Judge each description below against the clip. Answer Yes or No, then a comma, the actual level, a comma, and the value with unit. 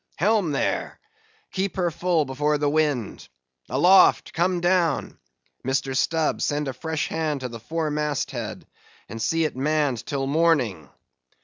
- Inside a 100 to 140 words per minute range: Yes, slow, 135 wpm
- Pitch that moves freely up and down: No, average, 4.1 semitones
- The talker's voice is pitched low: No, medium, 150 Hz